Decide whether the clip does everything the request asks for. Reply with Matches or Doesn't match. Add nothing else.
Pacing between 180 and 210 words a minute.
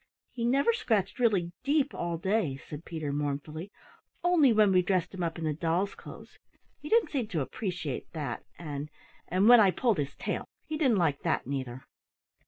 Matches